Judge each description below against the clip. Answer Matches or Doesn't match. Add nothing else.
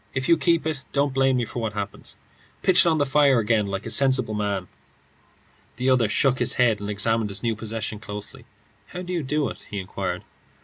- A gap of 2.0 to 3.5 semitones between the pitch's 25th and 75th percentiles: Doesn't match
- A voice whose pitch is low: Matches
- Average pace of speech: Doesn't match